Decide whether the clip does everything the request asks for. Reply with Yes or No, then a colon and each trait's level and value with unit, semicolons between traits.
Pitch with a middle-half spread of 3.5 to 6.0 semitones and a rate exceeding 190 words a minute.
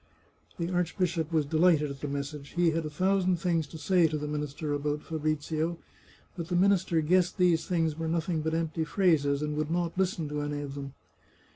No: average, 2.7 semitones; average, 200 wpm